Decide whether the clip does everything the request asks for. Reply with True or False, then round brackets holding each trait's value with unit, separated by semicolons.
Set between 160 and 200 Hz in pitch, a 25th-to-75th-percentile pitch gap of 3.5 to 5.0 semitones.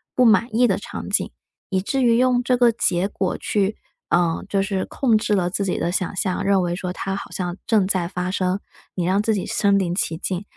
False (195 Hz; 2.9 semitones)